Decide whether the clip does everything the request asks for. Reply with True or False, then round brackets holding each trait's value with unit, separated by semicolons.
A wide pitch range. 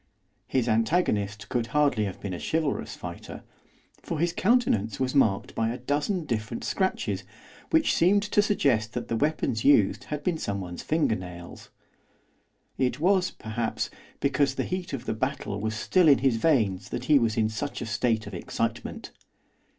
True (6.0 semitones)